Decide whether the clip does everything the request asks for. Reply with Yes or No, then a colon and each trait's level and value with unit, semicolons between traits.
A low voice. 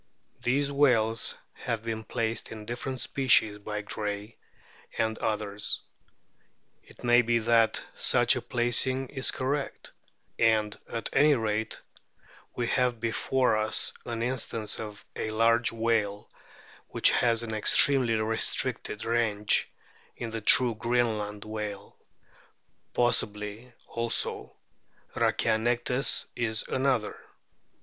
Yes: low, 115 Hz